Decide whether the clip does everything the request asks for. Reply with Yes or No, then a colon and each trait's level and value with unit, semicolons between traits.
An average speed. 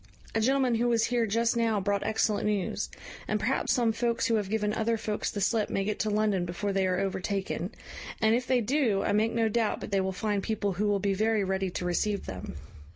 No: fast, 230 wpm